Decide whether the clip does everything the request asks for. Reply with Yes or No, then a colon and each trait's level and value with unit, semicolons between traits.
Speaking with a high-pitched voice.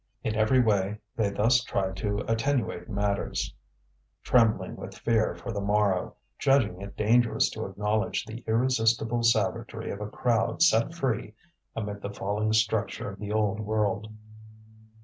No: low, 110 Hz